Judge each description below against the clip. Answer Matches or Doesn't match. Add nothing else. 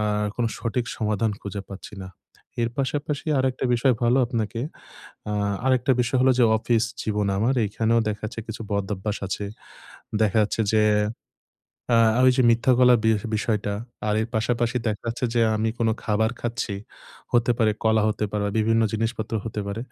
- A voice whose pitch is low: Matches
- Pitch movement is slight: Matches